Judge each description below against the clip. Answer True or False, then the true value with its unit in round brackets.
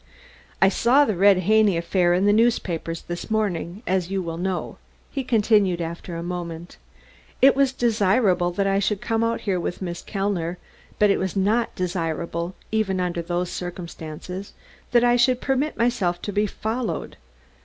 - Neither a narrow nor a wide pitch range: True (3.9 semitones)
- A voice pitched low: False (190 Hz)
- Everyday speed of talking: True (165 wpm)